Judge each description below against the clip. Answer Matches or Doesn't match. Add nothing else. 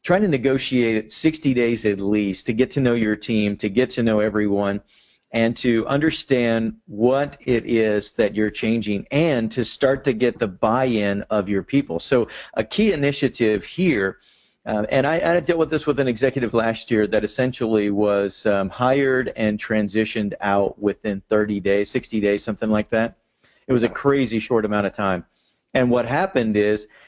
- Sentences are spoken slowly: Doesn't match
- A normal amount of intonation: Matches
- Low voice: Matches